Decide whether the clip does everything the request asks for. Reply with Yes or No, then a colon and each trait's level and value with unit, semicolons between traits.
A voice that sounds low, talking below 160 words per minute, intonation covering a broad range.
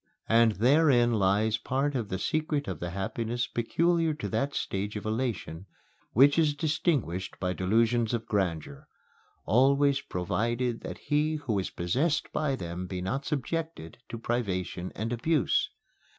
Yes: low, 120 Hz; average, 145 wpm; wide, 6.8 semitones